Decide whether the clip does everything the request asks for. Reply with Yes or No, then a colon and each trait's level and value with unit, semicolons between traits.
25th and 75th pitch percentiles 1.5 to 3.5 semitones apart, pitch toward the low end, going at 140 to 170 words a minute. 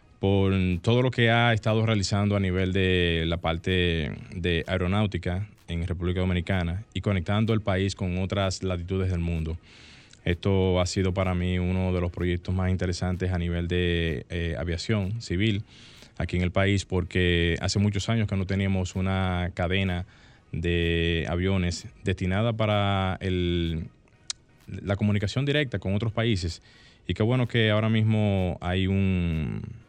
Yes: average, 2.8 semitones; very low, 95 Hz; average, 150 wpm